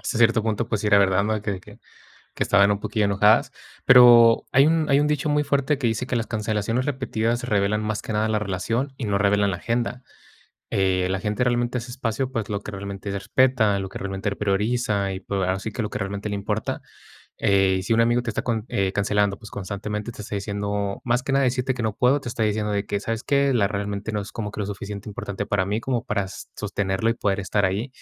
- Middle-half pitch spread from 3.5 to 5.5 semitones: No, average, 3.0 semitones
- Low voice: Yes, low, 105 Hz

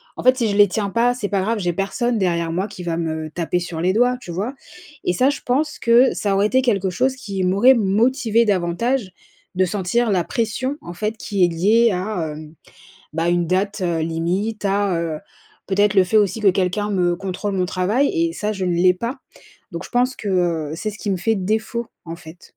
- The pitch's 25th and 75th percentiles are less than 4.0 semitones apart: No, average, 4.5 semitones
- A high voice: Yes, high, 200 Hz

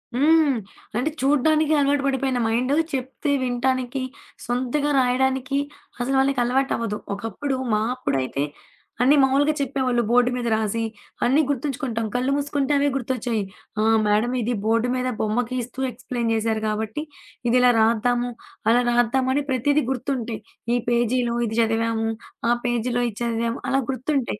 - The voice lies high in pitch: Yes, very high, 250 Hz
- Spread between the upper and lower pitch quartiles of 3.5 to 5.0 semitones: No, average, 2.8 semitones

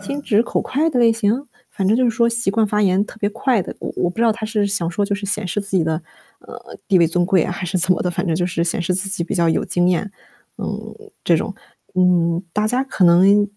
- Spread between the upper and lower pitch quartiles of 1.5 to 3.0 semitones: No, average, 3.7 semitones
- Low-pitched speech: No, high, 200 Hz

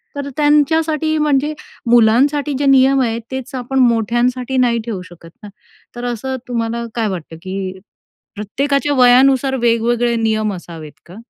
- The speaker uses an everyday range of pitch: Yes, average, 3.5 semitones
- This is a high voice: Yes, high, 245 Hz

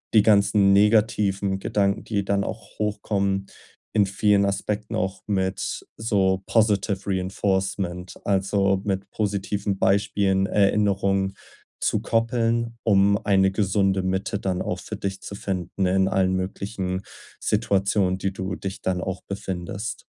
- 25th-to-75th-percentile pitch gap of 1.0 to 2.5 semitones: Yes, narrow, 1.3 semitones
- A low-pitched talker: Yes, low, 100 Hz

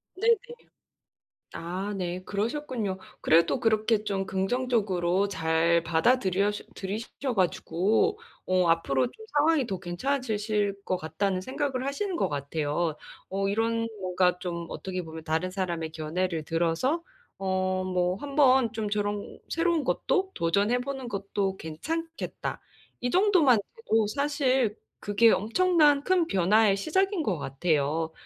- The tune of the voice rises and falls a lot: Yes, wide, 6.4 semitones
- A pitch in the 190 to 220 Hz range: Yes, high, 200 Hz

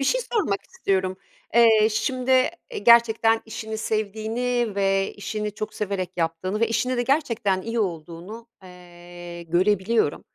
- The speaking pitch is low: No, high, 215 Hz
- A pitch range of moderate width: Yes, average, 3.7 semitones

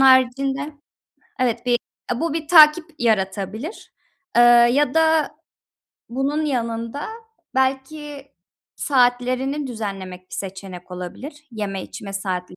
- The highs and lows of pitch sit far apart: Yes, wide, 5.8 semitones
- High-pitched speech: Yes, very high, 250 Hz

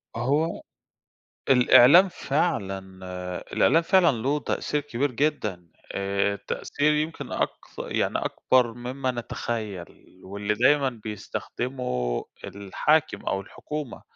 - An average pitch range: No, wide, 6.4 semitones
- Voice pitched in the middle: No, low, 125 Hz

